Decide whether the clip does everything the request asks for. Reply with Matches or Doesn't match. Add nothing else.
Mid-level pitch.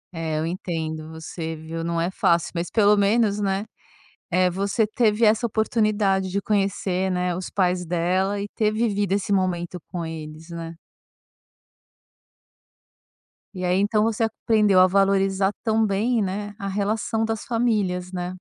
Doesn't match